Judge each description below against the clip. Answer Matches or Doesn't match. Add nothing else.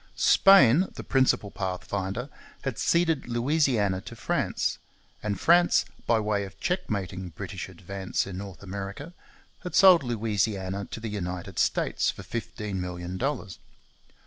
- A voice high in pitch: Doesn't match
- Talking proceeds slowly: Matches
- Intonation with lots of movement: Matches